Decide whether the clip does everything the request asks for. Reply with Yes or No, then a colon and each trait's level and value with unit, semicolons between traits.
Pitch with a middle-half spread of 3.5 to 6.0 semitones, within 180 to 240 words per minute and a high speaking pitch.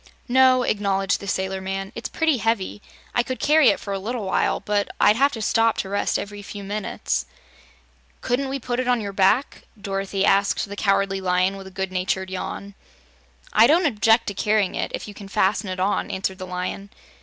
No: average, 3.0 semitones; average, 200 wpm; high, 200 Hz